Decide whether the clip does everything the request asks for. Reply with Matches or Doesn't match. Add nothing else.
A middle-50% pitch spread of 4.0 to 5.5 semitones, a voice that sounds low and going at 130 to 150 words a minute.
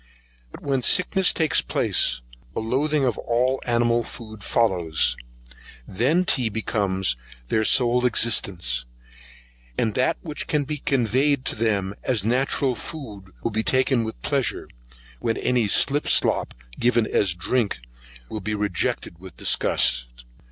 Matches